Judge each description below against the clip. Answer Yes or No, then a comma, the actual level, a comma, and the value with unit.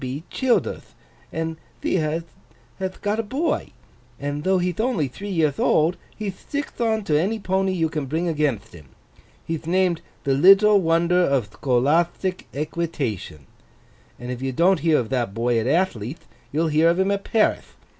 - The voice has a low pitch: No, medium, 165 Hz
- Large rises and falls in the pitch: Yes, wide, 5.7 semitones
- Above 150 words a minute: Yes, average, 170 wpm